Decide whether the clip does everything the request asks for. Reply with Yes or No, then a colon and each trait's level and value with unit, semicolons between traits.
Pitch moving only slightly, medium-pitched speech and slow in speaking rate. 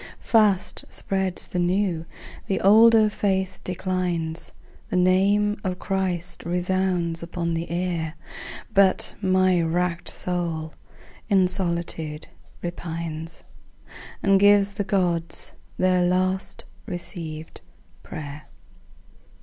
Yes: narrow, 2.2 semitones; medium, 180 Hz; slow, 95 wpm